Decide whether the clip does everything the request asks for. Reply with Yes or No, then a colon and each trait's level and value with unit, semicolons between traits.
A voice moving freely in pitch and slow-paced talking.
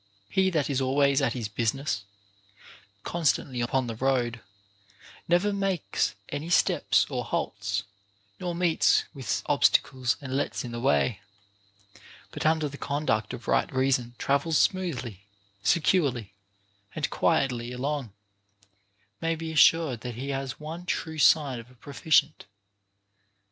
No: average, 4.7 semitones; slow, 130 wpm